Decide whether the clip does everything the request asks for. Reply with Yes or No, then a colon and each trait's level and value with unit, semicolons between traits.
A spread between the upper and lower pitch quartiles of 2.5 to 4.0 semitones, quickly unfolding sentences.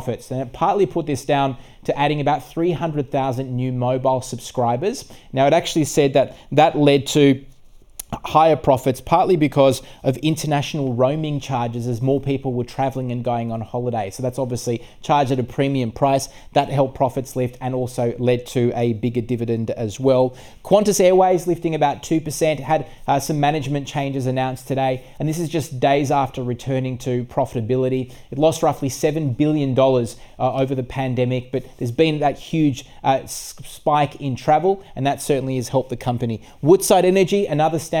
No: average, 2.9 semitones; average, 175 wpm